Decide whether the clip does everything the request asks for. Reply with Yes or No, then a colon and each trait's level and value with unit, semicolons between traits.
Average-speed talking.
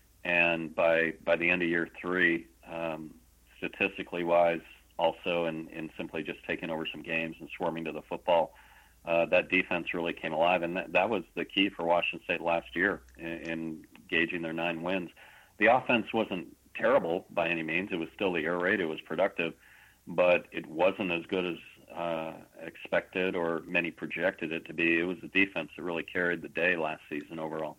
Yes: average, 195 wpm